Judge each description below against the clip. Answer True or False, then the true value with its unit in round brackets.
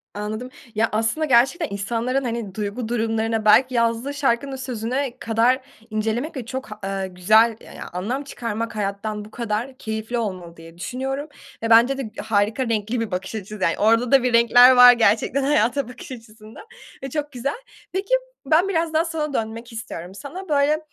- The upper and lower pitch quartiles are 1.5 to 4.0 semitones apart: True (3.7 semitones)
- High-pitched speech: True (235 Hz)